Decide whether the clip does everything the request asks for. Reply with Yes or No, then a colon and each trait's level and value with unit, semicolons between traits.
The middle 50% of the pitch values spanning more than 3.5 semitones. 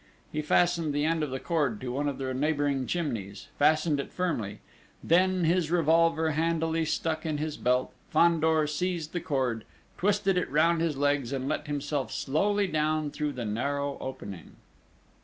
No: average, 3.2 semitones